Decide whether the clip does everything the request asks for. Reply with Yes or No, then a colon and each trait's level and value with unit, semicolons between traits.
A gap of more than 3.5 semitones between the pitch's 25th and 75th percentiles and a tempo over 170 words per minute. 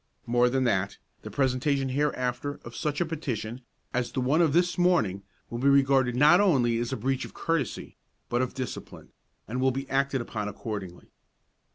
No: average, 3.1 semitones; average, 180 wpm